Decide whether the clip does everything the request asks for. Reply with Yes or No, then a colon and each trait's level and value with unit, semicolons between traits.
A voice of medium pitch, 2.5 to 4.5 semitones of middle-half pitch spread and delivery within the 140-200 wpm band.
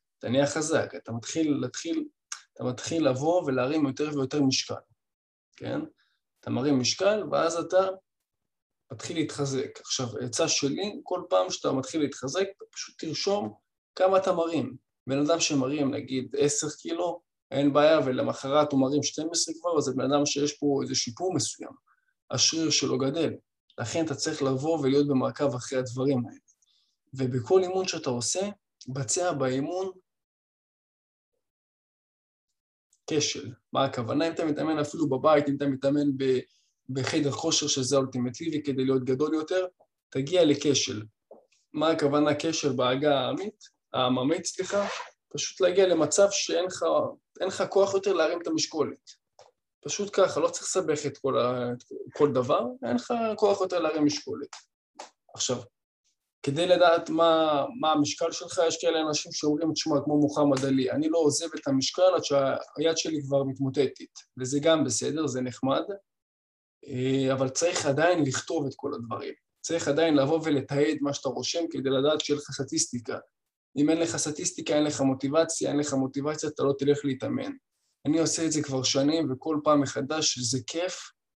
Yes: medium, 150 Hz; average, 3.6 semitones; average, 145 wpm